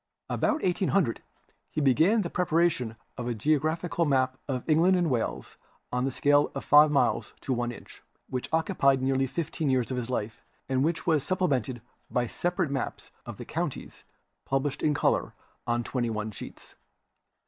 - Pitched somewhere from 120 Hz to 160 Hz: Yes, medium, 140 Hz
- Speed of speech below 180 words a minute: Yes, average, 165 wpm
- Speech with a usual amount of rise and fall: Yes, average, 4.5 semitones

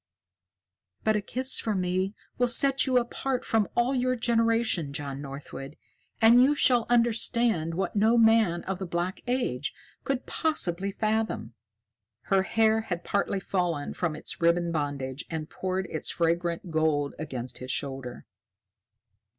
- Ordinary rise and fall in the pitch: No, wide, 6.4 semitones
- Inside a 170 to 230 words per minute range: No, average, 140 wpm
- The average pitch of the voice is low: No, high, 190 Hz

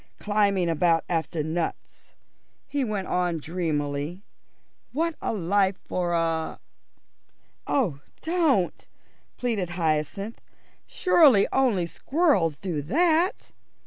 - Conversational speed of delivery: No, slow, 100 wpm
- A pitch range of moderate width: No, wide, 7.1 semitones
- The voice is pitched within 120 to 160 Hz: No, medium, 185 Hz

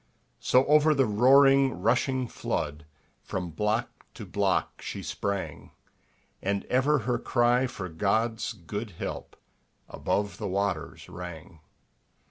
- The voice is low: Yes, low, 105 Hz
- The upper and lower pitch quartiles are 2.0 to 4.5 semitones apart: No, average, 5.3 semitones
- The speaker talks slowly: Yes, slow, 115 wpm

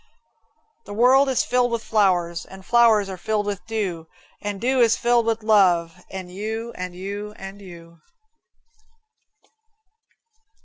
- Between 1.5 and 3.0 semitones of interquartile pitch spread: No, average, 3.7 semitones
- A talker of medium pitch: No, high, 205 Hz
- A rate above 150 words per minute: No, slow, 135 wpm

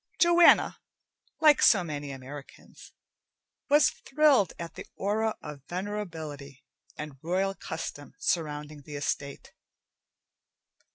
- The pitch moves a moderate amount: No, wide, 6.1 semitones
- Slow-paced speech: Yes, slow, 100 wpm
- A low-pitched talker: No, medium, 165 Hz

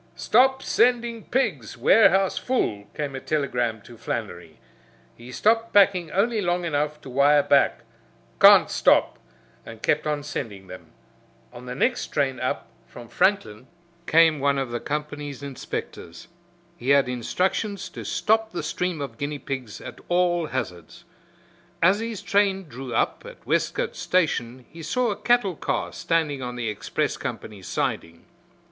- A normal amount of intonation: No, wide, 7.5 semitones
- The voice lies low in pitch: No, medium, 145 Hz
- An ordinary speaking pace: Yes, average, 150 wpm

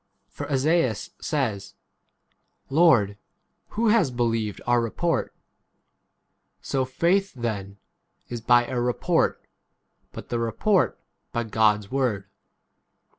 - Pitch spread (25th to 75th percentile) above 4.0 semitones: Yes, average, 5.3 semitones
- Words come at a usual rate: No, slow, 110 wpm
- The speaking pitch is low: Yes, low, 120 Hz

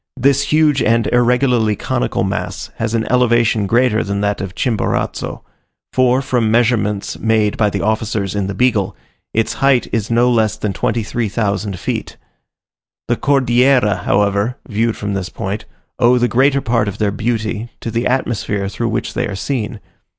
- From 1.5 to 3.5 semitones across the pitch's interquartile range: Yes, average, 3.0 semitones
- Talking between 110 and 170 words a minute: Yes, average, 160 wpm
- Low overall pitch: Yes, low, 115 Hz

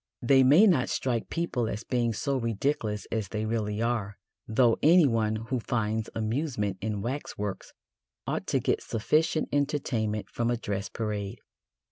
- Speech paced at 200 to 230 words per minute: No, average, 145 wpm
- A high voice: No, low, 115 Hz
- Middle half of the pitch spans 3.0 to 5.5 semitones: Yes, average, 3.8 semitones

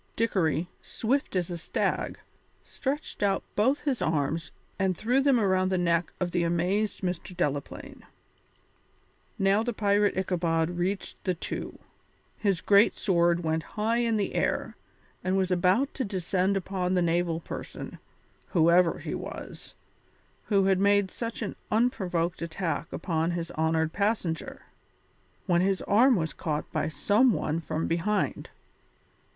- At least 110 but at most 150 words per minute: Yes, average, 140 wpm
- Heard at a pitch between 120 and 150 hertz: No, medium, 185 Hz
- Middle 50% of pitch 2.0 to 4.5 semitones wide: Yes, average, 3.5 semitones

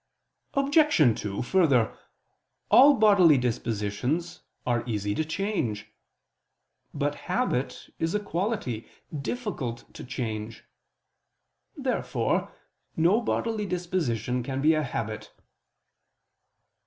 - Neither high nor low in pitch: Yes, medium, 150 Hz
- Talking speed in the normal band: No, slow, 95 wpm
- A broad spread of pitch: Yes, wide, 8.9 semitones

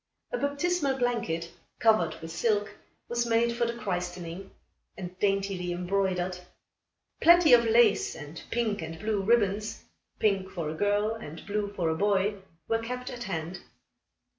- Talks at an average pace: Yes, average, 145 wpm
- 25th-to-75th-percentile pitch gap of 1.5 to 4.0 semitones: No, average, 4.7 semitones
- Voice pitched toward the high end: Yes, high, 205 Hz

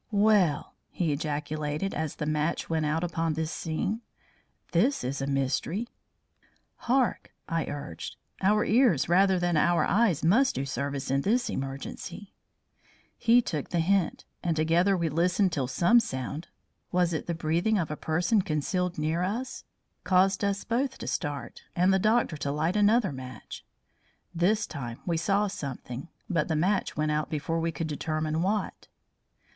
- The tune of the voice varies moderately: Yes, average, 4.5 semitones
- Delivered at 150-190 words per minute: Yes, average, 160 wpm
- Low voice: No, medium, 165 Hz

